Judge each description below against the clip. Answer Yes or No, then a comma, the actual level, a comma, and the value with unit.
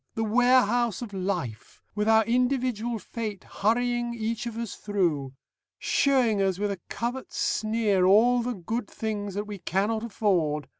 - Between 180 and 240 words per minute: No, average, 150 wpm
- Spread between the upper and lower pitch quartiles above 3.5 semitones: No, average, 3.2 semitones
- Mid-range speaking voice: No, high, 220 Hz